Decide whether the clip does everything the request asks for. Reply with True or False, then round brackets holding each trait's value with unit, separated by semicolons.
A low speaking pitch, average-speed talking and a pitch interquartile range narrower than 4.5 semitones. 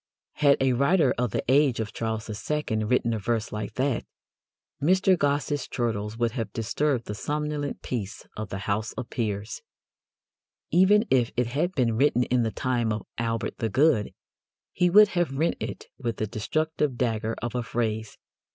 False (120 Hz; 170 wpm; 4.8 semitones)